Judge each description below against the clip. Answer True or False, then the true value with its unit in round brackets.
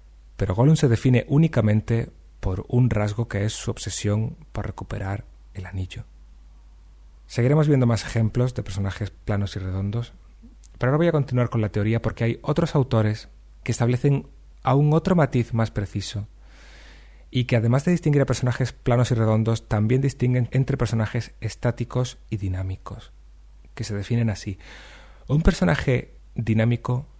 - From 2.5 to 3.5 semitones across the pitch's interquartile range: False (4.2 semitones)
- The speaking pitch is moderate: False (115 Hz)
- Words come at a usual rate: True (150 wpm)